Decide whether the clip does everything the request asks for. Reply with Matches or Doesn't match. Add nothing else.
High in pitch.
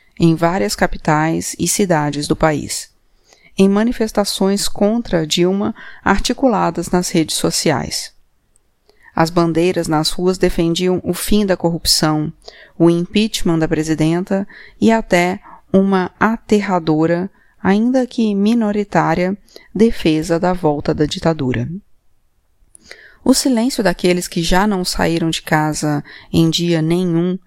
Doesn't match